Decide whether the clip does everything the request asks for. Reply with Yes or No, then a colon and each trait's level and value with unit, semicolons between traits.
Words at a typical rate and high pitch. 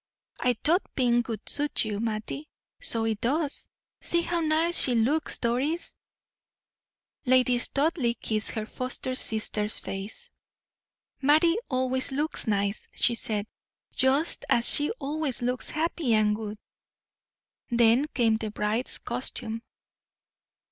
No: slow, 120 wpm; very high, 250 Hz